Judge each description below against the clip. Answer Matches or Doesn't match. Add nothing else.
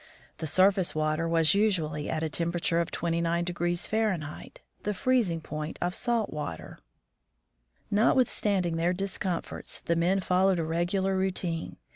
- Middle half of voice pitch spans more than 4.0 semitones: Doesn't match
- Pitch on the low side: Doesn't match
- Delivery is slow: Matches